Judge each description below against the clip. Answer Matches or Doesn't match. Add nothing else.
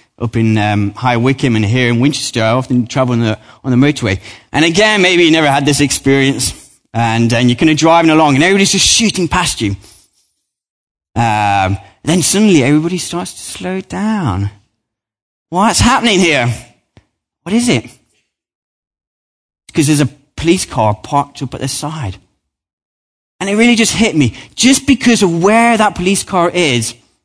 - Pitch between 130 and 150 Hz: Matches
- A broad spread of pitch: Matches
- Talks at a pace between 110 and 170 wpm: Matches